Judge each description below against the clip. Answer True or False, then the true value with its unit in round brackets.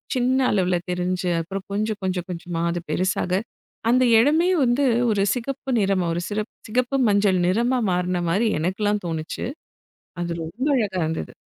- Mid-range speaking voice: False (195 Hz)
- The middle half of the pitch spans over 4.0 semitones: True (4.8 semitones)